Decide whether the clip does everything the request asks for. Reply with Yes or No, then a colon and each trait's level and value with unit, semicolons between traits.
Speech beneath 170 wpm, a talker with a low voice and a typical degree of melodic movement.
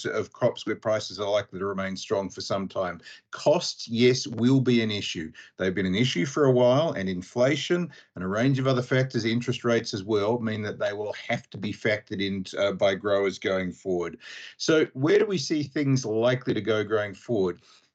No: fast, 205 wpm; low, 115 Hz; average, 4.7 semitones